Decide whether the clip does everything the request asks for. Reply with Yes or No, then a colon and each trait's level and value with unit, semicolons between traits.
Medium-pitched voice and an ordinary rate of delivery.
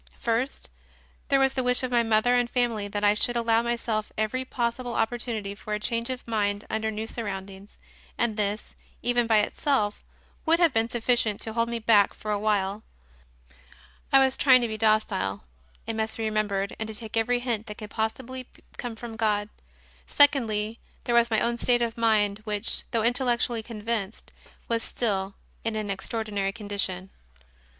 No: high, 225 Hz; average, 175 wpm